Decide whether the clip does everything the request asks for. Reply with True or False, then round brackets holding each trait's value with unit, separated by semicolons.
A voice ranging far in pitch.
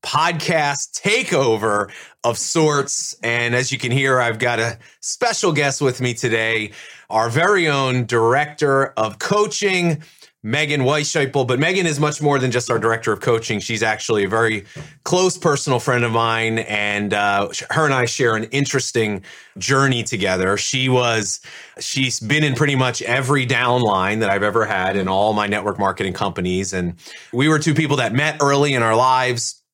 False (4.4 semitones)